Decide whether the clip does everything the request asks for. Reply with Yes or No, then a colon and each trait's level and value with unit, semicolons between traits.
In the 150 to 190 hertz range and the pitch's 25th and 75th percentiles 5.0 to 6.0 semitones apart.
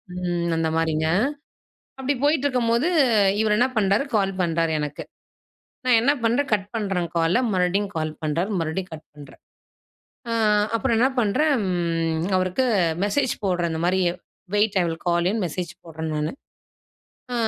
Yes: medium, 185 Hz; wide, 5.4 semitones